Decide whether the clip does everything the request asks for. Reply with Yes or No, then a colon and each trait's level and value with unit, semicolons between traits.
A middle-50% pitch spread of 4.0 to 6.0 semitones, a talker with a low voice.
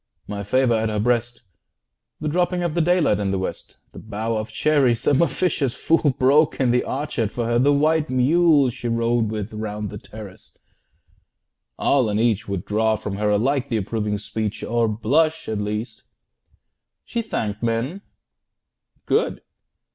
Yes: average, 5.1 semitones; low, 120 Hz